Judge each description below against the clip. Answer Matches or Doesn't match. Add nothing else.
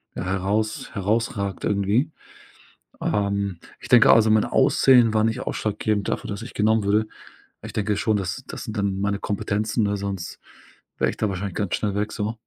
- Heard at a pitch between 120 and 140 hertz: Doesn't match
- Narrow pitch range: Matches